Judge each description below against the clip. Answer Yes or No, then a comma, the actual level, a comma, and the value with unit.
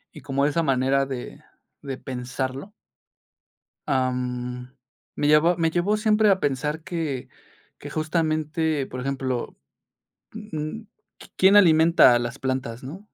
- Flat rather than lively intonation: No, average, 4.2 semitones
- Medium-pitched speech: Yes, medium, 145 Hz